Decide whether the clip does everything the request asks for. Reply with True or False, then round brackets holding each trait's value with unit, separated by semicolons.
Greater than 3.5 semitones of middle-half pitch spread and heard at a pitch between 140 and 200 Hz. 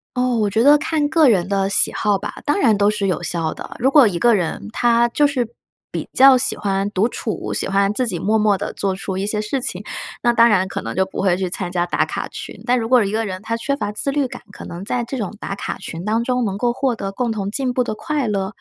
False (4.2 semitones; 215 Hz)